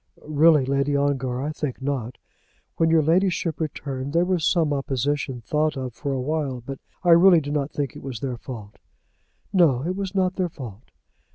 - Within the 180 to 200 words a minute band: Yes, average, 185 wpm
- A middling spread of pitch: Yes, average, 3.7 semitones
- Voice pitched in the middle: Yes, medium, 145 Hz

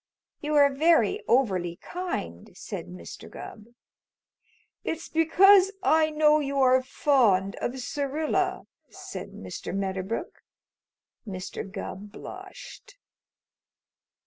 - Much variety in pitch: Yes, wide, 8.2 semitones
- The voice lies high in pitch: Yes, very high, 275 Hz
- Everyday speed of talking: No, slow, 95 wpm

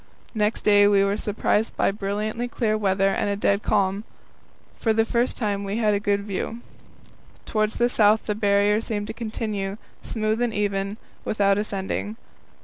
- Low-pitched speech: No, high, 210 Hz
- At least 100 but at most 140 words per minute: No, average, 165 wpm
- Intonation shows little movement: Yes, narrow, 1.4 semitones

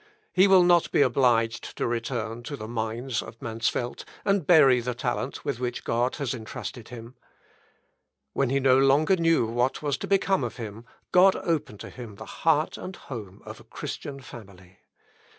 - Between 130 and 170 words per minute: No, average, 180 wpm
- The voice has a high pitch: No, low, 125 Hz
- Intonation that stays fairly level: No, average, 4.1 semitones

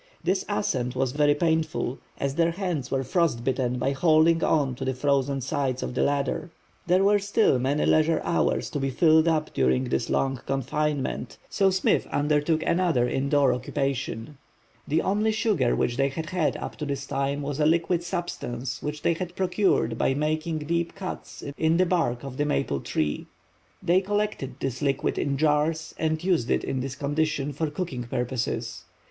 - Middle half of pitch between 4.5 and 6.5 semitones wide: No, average, 3.8 semitones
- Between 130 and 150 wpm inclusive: No, average, 175 wpm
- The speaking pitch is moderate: Yes, medium, 145 Hz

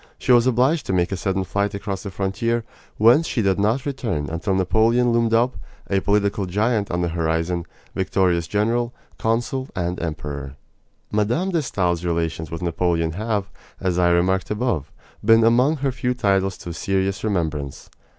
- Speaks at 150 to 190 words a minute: Yes, average, 165 wpm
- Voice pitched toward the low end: Yes, low, 100 Hz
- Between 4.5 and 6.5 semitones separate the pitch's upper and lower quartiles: Yes, average, 4.9 semitones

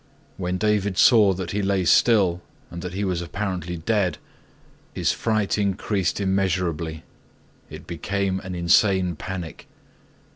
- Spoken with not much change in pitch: Yes, narrow, 2.3 semitones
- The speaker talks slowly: Yes, slow, 125 wpm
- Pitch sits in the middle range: No, very low, 95 Hz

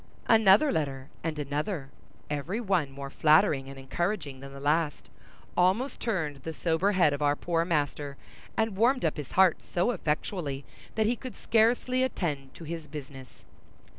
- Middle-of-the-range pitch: Yes, medium, 160 Hz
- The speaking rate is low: No, average, 160 wpm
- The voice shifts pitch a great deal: Yes, wide, 5.7 semitones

